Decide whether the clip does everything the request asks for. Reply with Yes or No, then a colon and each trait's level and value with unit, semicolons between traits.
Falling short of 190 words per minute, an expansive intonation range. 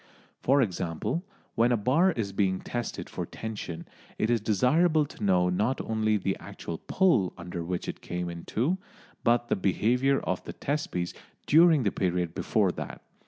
Yes: average, 170 wpm; wide, 6.7 semitones